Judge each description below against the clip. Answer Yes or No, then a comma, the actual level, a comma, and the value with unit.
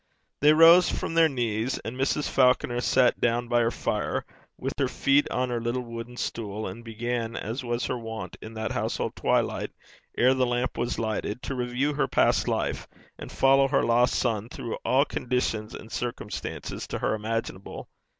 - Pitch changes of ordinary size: No, narrow, 2.2 semitones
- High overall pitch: No, low, 120 Hz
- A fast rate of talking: No, average, 180 wpm